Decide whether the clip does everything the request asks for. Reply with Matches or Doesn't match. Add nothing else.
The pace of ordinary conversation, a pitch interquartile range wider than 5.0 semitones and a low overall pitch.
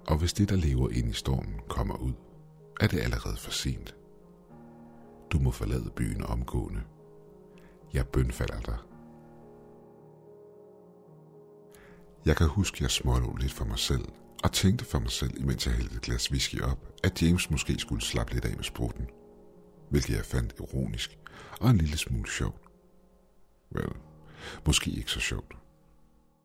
Matches